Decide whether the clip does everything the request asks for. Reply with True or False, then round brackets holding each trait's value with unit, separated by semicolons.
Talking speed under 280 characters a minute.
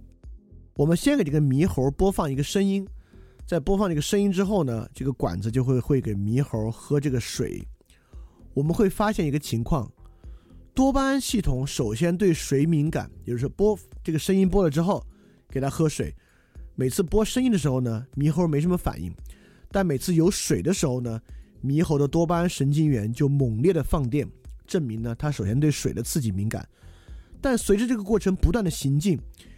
False (285 characters per minute)